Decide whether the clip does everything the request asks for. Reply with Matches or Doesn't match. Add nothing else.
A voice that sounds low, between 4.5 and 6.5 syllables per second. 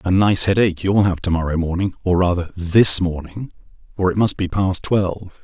Matches